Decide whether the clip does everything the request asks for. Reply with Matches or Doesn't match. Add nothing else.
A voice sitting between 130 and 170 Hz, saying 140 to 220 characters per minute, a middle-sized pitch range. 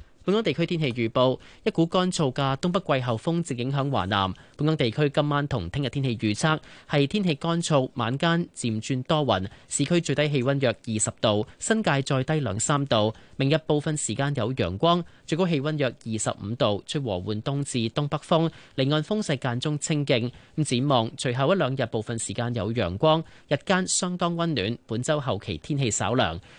Doesn't match